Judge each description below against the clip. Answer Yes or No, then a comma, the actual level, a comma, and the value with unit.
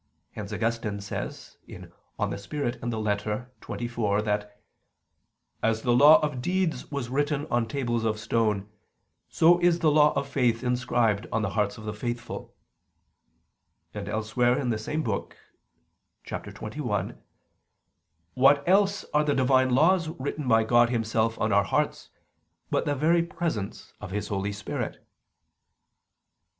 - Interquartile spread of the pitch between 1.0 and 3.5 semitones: No, average, 5.0 semitones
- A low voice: Yes, low, 120 Hz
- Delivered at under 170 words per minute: Yes, average, 140 wpm